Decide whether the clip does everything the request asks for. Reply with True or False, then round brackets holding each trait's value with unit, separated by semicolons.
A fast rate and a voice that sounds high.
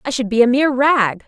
True (280 wpm; 250 Hz)